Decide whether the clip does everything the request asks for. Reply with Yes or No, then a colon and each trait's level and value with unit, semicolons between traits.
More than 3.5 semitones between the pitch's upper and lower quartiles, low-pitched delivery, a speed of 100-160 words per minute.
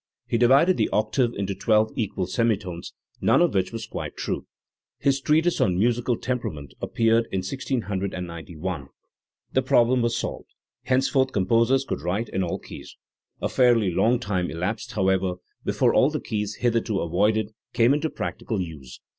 Yes: average, 4.7 semitones; low, 110 Hz; average, 155 wpm